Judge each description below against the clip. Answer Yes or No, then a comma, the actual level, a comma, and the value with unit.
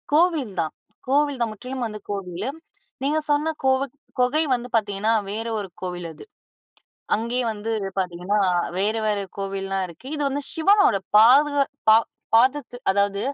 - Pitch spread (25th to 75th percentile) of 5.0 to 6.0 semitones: Yes, wide, 5.6 semitones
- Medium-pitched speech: No, high, 225 Hz